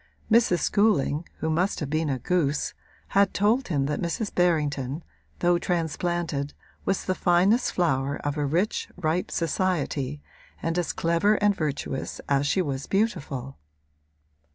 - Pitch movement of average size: Yes, average, 4.5 semitones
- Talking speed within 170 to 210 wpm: No, average, 140 wpm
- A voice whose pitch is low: No, medium, 165 Hz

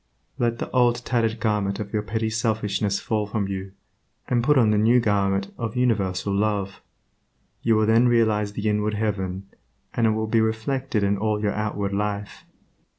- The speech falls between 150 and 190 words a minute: Yes, average, 175 wpm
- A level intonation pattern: Yes, narrow, 2.0 semitones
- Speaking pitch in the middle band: No, low, 105 Hz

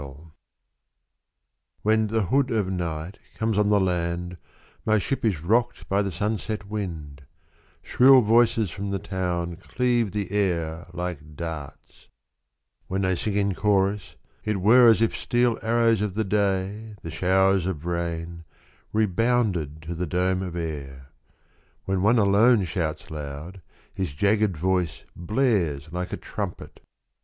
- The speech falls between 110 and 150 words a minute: Yes, average, 140 wpm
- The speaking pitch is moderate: No, very low, 95 Hz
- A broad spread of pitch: No, average, 4.0 semitones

